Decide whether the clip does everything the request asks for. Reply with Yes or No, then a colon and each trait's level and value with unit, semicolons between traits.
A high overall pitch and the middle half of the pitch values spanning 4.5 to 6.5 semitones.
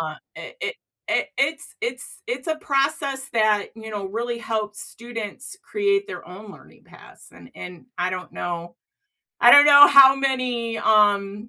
Yes: high, 230 Hz; average, 5.2 semitones